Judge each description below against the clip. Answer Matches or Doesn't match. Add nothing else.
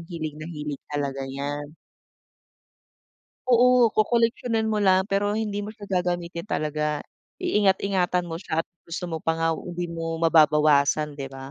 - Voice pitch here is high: Doesn't match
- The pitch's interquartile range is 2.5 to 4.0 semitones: Doesn't match